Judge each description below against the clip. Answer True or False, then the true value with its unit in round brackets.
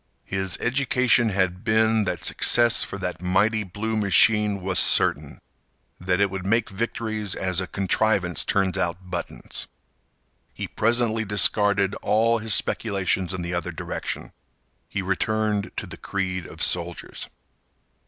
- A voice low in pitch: True (100 Hz)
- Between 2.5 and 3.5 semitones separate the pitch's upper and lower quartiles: True (2.9 semitones)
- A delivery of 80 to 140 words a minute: True (135 wpm)